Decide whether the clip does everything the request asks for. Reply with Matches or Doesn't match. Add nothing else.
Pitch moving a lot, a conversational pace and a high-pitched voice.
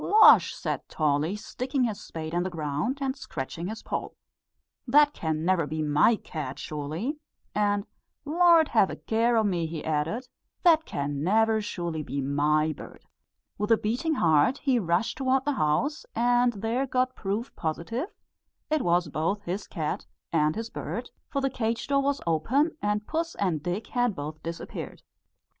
Matches